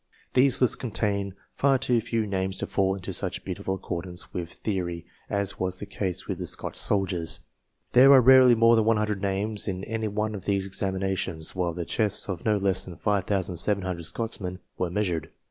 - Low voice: Yes, low, 100 Hz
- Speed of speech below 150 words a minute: No, average, 180 wpm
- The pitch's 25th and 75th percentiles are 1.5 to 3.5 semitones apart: Yes, average, 2.8 semitones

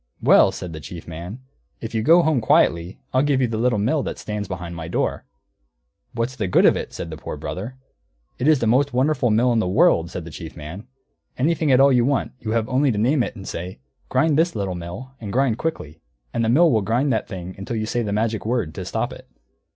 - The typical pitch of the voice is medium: No, low, 115 Hz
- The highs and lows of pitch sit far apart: Yes, wide, 5.8 semitones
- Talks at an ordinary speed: No, fast, 245 wpm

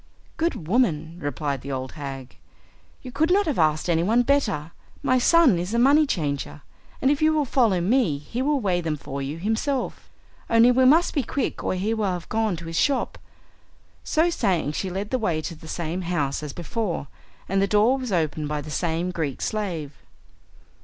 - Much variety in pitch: Yes, wide, 8.3 semitones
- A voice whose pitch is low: No, medium, 185 Hz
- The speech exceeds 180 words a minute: Yes, average, 195 wpm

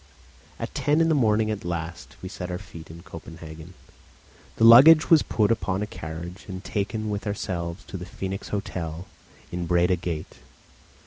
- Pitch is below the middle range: Yes, very low, 95 Hz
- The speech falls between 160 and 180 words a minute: Yes, average, 170 wpm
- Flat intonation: No, average, 3.9 semitones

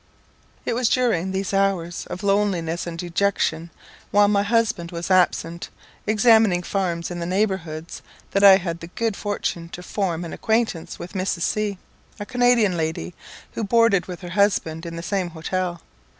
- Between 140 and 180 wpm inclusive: Yes, average, 165 wpm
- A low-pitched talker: No, medium, 185 Hz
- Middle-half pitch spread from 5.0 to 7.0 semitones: No, average, 3.3 semitones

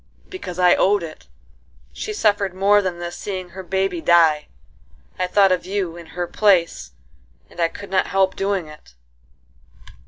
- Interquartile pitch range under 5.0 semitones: Yes, narrow, 2.4 semitones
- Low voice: No, medium, 185 Hz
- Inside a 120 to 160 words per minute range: Yes, average, 150 wpm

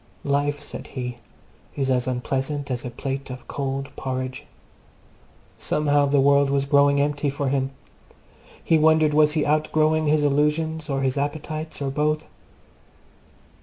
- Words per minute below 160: Yes, average, 140 wpm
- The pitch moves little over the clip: Yes, narrow, 1.9 semitones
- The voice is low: No, medium, 145 Hz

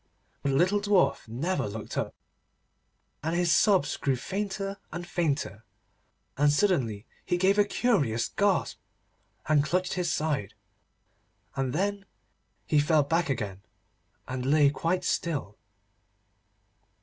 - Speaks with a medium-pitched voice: Yes, medium, 160 Hz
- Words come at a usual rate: No, slow, 125 wpm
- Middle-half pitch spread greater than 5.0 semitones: Yes, wide, 5.6 semitones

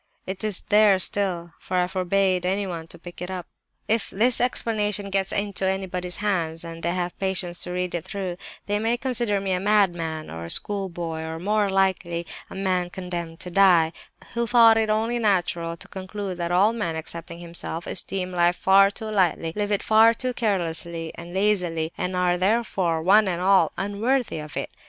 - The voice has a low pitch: No, medium, 185 Hz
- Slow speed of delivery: No, average, 185 wpm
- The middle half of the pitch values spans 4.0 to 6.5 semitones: No, average, 3.0 semitones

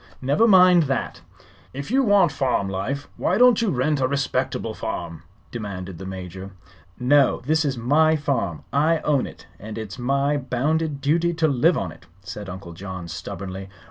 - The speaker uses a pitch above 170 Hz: No, low, 135 Hz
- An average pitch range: No, wide, 8.2 semitones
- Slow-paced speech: No, average, 170 wpm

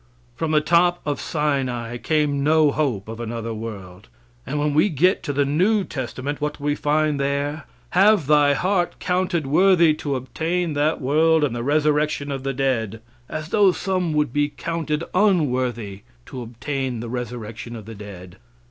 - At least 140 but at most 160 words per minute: No, average, 170 wpm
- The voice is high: No, medium, 145 Hz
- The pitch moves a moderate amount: Yes, average, 4.4 semitones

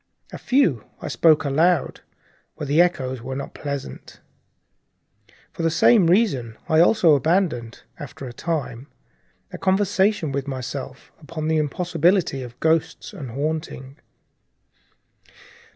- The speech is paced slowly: Yes, slow, 120 wpm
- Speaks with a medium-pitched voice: Yes, medium, 155 Hz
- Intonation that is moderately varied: Yes, average, 4.4 semitones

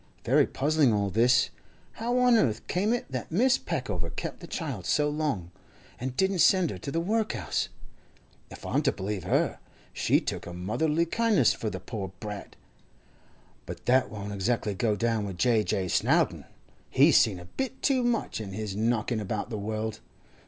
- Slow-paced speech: No, average, 175 wpm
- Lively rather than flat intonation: Yes, wide, 8.1 semitones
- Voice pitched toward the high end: No, low, 115 Hz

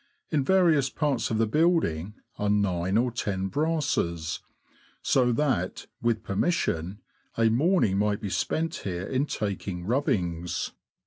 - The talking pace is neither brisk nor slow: No, slow, 130 wpm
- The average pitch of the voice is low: Yes, low, 110 Hz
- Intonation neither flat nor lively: No, wide, 7.2 semitones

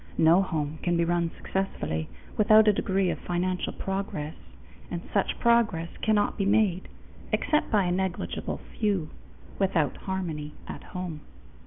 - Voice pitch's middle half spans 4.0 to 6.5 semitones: No, average, 3.3 semitones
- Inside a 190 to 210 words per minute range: No, average, 140 wpm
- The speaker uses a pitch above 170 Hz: Yes, medium, 185 Hz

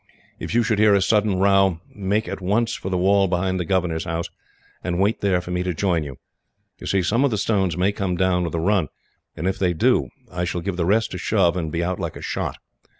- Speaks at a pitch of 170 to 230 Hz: No, very low, 95 Hz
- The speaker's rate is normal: No, fast, 250 wpm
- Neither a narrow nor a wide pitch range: No, narrow, 2.3 semitones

